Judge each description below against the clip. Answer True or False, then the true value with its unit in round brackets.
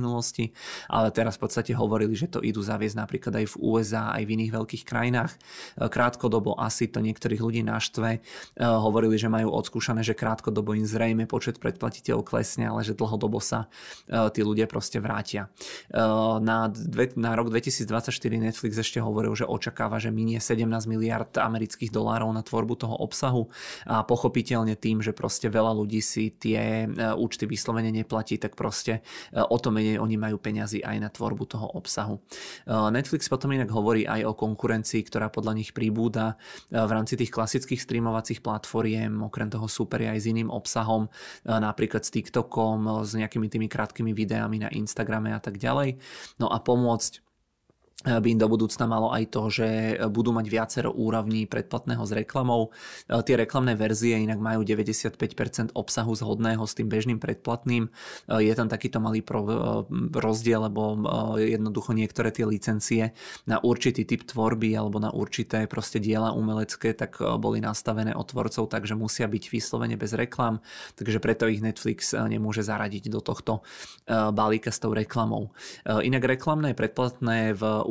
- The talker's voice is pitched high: False (110 Hz)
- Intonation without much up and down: True (1.2 semitones)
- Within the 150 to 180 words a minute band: True (155 wpm)